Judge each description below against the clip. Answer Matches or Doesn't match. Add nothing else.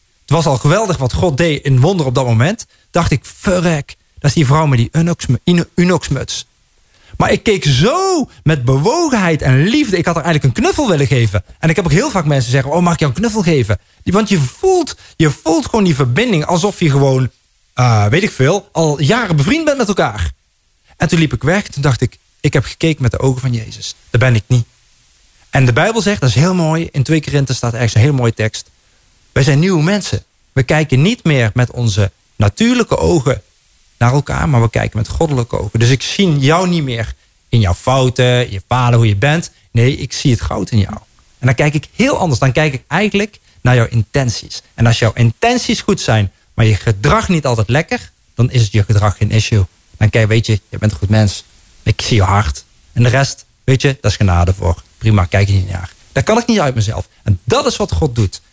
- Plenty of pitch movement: Matches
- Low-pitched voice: Matches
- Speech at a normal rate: Doesn't match